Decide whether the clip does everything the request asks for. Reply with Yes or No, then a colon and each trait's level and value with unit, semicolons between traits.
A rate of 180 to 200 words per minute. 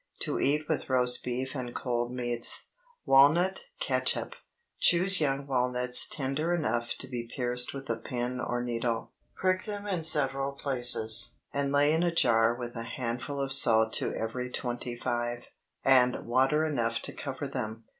No: average, 160 wpm